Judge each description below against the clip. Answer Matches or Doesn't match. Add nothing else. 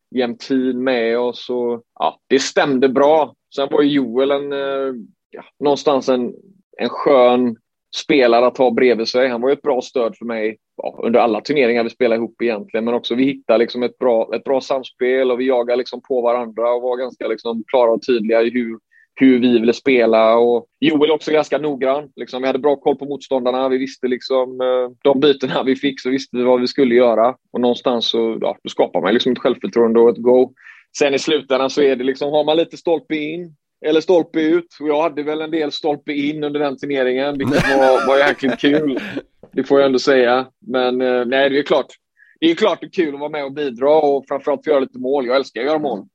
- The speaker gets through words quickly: Matches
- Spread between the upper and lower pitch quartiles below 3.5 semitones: Matches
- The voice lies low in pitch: Matches